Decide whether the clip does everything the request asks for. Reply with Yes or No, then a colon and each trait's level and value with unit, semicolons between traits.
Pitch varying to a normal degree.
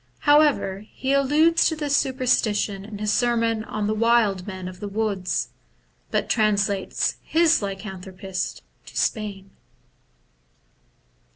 Yes: average, 4.7 semitones